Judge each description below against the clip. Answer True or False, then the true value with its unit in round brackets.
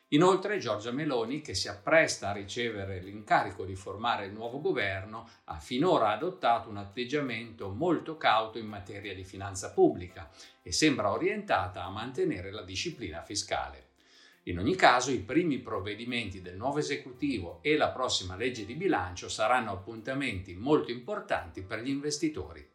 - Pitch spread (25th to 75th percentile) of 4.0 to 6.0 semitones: True (5.0 semitones)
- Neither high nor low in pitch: False (115 Hz)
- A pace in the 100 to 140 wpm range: False (150 wpm)